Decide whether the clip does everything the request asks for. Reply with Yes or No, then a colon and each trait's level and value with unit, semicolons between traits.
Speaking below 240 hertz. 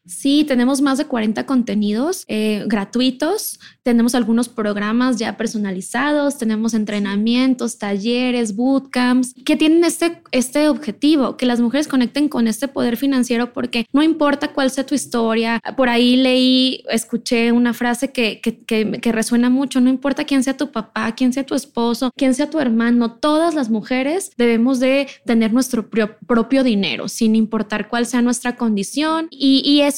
No: high, 245 Hz